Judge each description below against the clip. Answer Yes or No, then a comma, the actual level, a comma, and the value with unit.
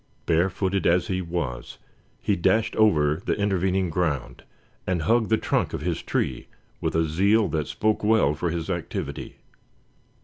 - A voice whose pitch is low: Yes, very low, 90 Hz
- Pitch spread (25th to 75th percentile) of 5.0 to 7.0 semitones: No, average, 3.8 semitones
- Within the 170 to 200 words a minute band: No, average, 150 wpm